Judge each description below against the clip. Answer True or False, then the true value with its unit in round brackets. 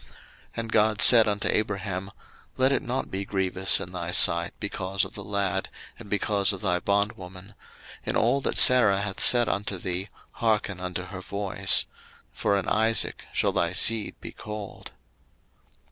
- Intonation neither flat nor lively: False (2.3 semitones)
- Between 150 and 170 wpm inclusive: True (160 wpm)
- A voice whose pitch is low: True (100 Hz)